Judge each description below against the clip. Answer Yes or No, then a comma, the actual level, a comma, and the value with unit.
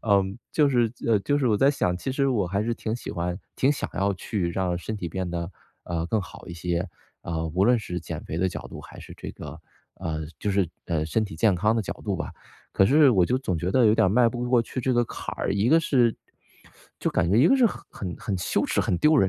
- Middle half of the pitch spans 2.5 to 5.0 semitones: No, wide, 5.6 semitones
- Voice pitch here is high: No, low, 100 Hz